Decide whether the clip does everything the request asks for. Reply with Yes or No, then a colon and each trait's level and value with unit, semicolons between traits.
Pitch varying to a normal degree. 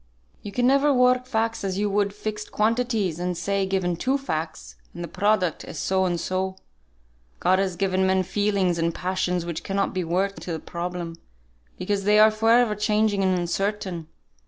Yes: average, 3.1 semitones